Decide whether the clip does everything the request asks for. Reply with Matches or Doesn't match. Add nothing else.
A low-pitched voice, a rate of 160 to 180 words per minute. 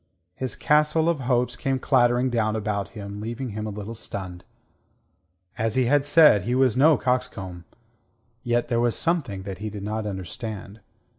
Matches